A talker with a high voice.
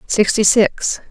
Yes: high, 210 Hz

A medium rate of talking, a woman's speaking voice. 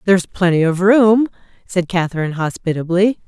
No: slow, 130 wpm; female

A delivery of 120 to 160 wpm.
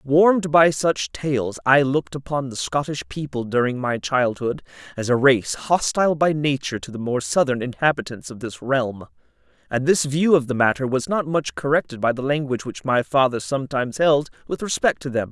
No: average, 190 wpm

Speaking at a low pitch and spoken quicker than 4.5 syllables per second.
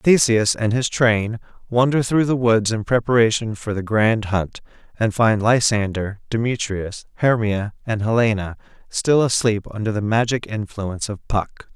No: low, 110 Hz; 4.4 syllables/s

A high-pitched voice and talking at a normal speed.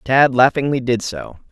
No: low, 125 Hz; average, 160 wpm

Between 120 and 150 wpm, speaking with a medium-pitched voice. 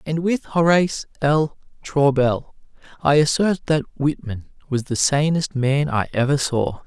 Yes: average, 140 wpm; medium, 145 Hz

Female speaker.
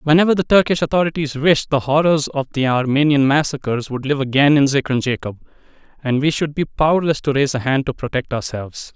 No: male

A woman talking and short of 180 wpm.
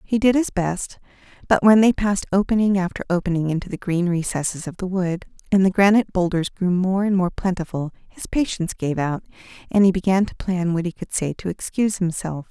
No: female; fast, 205 wpm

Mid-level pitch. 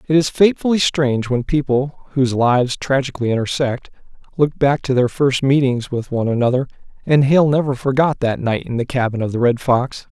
No: low, 130 Hz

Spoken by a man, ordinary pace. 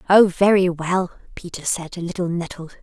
No: female; average, 170 wpm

